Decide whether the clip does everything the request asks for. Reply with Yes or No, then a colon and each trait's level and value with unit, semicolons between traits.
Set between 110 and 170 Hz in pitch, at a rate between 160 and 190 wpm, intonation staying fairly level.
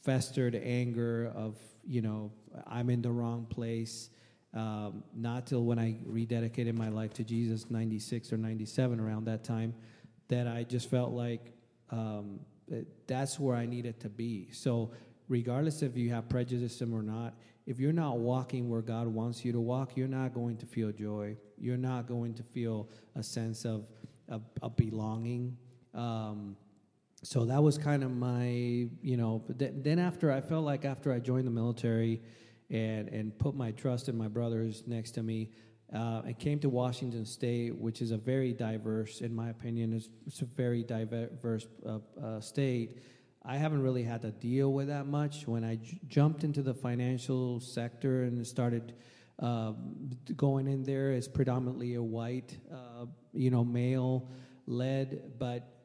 Yes: low, 120 Hz; average, 170 wpm; narrow, 2.1 semitones